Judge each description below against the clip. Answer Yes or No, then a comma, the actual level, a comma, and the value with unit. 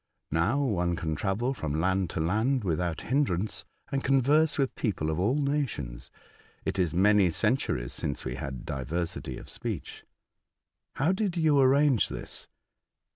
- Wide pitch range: Yes, wide, 8.9 semitones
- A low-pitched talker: Yes, low, 100 Hz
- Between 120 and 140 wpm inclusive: No, average, 150 wpm